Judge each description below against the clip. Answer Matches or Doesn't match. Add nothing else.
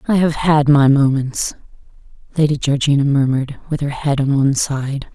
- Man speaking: Doesn't match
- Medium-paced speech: Matches